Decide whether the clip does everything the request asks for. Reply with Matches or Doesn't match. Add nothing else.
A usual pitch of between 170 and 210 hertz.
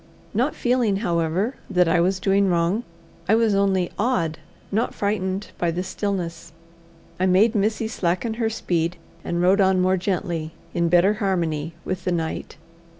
Matches